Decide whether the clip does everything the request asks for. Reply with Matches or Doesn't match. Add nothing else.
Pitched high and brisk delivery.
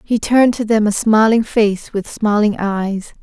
Doesn't match